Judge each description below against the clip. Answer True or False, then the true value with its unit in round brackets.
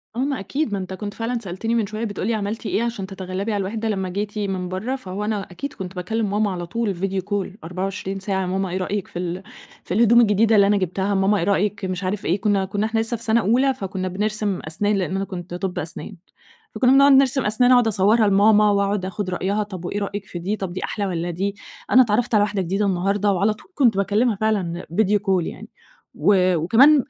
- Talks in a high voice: True (200 Hz)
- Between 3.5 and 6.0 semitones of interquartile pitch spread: False (2.5 semitones)